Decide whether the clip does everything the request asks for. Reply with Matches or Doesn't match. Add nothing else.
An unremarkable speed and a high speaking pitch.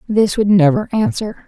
Matches